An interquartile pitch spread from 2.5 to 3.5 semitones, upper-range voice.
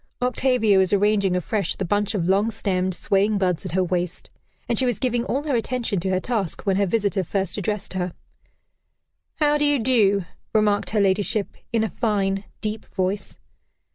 Yes: average, 2.9 semitones; high, 205 Hz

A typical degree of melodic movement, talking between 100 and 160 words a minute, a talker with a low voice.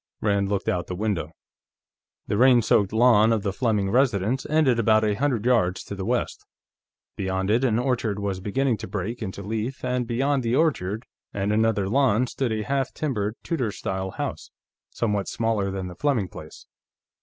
No: average, 3.9 semitones; average, 180 wpm; low, 110 Hz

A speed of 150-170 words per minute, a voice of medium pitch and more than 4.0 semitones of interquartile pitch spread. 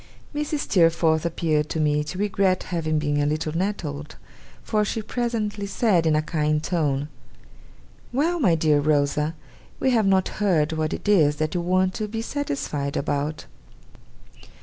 Yes: average, 155 wpm; medium, 165 Hz; average, 5.2 semitones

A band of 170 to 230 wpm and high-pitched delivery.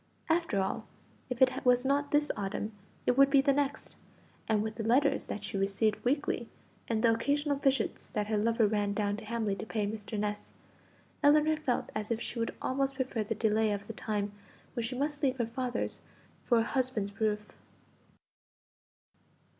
Yes: average, 180 wpm; high, 230 Hz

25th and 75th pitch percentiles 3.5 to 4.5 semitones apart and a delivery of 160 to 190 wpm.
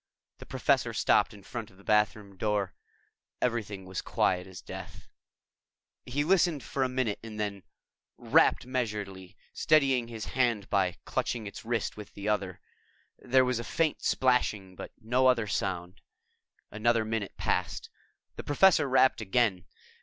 No: average, 4.2 semitones; average, 145 wpm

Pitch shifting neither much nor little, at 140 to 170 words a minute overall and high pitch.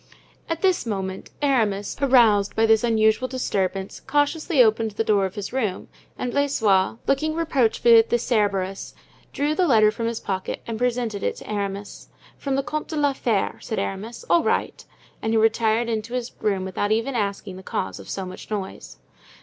No: average, 4.2 semitones; average, 180 wpm; high, 225 Hz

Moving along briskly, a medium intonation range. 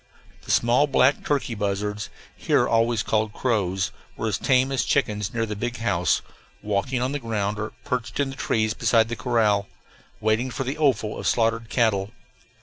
No: average, 180 wpm; average, 3.0 semitones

